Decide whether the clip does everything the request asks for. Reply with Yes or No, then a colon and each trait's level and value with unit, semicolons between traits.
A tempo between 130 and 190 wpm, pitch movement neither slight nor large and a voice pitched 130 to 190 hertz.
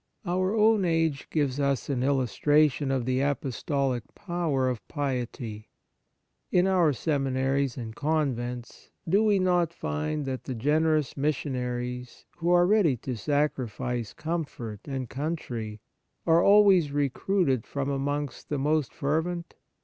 Yes: slow, 135 wpm; average, 4.4 semitones; medium, 140 Hz